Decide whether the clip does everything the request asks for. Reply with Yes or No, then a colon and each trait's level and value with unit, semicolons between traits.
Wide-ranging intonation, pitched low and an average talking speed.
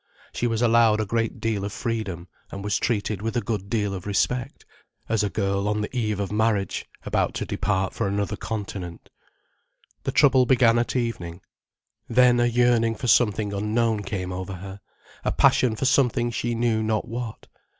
No: average, 2.8 semitones; low, 110 Hz; average, 180 wpm